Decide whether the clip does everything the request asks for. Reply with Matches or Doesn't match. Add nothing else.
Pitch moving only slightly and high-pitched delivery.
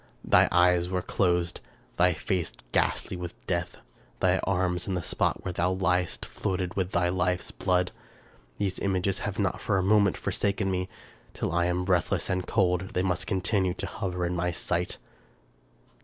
Doesn't match